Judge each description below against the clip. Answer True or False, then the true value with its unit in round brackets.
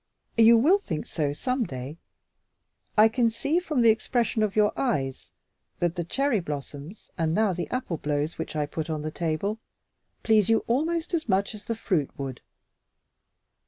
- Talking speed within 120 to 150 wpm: False (170 wpm)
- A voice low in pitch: False (205 Hz)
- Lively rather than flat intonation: True (7.1 semitones)